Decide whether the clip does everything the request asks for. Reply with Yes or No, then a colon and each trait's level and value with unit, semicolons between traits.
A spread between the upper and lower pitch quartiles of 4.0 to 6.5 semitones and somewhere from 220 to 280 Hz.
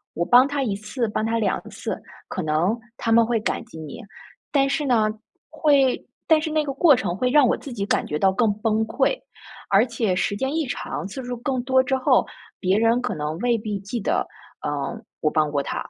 Yes: average, 4.8 semitones; high, 230 Hz